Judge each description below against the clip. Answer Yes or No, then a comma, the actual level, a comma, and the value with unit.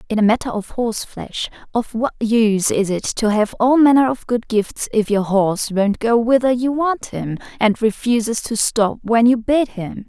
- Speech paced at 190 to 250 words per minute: Yes, average, 200 wpm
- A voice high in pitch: Yes, high, 225 Hz